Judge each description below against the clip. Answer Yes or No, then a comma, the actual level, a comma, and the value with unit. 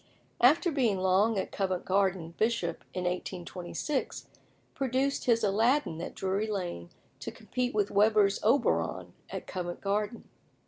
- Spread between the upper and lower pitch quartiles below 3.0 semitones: No, average, 4.1 semitones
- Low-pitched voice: No, high, 200 Hz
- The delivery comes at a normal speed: No, slow, 130 wpm